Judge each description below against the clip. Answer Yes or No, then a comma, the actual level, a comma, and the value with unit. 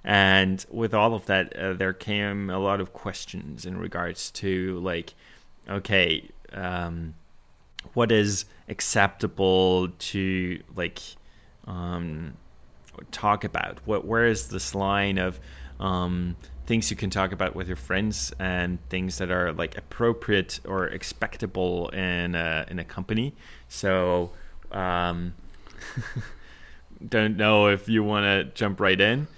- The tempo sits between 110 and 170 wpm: Yes, slow, 135 wpm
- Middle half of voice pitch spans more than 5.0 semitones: No, narrow, 2.4 semitones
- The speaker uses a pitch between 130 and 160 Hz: No, very low, 95 Hz